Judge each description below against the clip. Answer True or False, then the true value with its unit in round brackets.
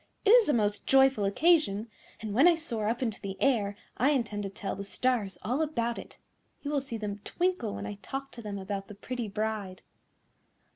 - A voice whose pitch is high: True (225 Hz)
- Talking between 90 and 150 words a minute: False (205 wpm)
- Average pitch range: True (4.9 semitones)